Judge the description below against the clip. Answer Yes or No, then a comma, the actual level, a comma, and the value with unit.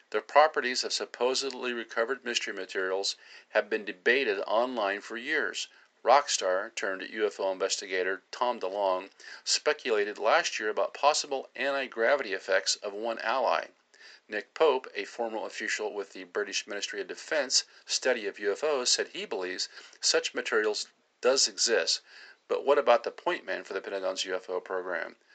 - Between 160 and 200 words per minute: No, average, 145 wpm